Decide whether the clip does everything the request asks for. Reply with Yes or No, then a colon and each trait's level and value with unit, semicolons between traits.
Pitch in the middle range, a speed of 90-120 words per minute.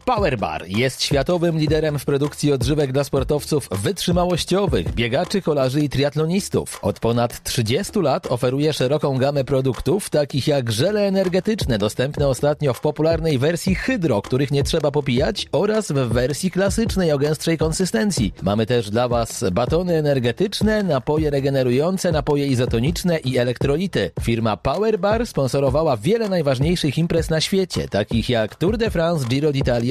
No: medium, 145 Hz; average, 140 wpm